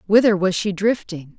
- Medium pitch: No, high, 195 Hz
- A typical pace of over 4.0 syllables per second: Yes, 4.9 syllables/s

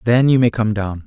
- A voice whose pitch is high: No, low, 110 Hz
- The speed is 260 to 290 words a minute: Yes, fast, 285 wpm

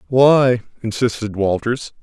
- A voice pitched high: No, low, 120 Hz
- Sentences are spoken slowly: Yes, slow, 90 wpm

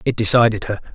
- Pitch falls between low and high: No, low, 110 Hz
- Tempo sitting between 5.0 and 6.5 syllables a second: No, 6.9 syllables/s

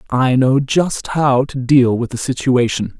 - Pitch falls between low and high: No, low, 130 Hz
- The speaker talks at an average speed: Yes, average, 180 wpm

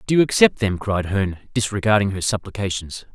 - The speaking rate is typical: Yes, average, 170 wpm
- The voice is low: Yes, low, 100 Hz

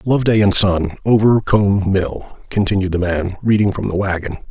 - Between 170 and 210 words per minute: No, average, 160 wpm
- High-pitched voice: No, low, 100 Hz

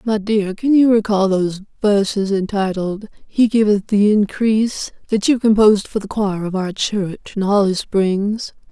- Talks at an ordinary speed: Yes, average, 165 wpm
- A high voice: Yes, high, 205 Hz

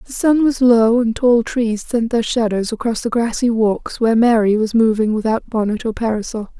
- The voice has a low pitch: No, high, 230 Hz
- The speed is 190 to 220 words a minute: Yes, average, 200 wpm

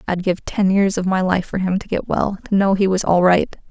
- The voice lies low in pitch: No, high, 190 Hz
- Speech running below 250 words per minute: No, fast, 290 wpm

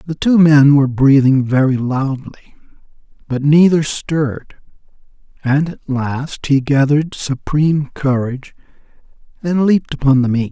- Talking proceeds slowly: Yes, slow, 125 wpm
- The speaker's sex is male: Yes, male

